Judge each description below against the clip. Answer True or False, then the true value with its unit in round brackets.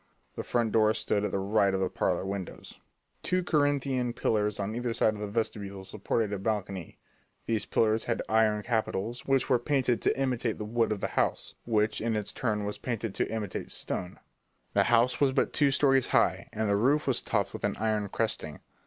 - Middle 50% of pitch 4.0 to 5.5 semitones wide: False (3.0 semitones)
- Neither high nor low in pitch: False (110 Hz)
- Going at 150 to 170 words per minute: False (200 wpm)